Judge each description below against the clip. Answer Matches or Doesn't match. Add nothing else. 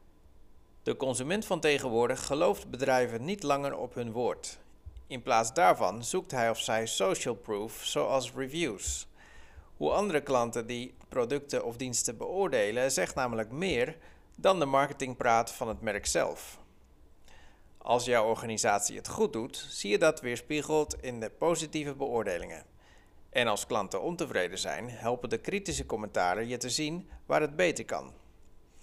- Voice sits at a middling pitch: Doesn't match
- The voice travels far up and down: Matches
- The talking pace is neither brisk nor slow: Matches